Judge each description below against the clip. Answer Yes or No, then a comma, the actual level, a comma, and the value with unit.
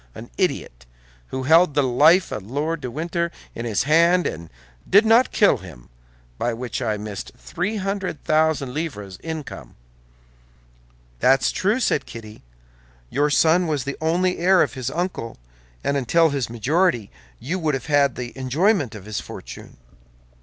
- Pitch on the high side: No, medium, 145 Hz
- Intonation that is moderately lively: No, wide, 6.1 semitones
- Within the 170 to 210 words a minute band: No, average, 155 wpm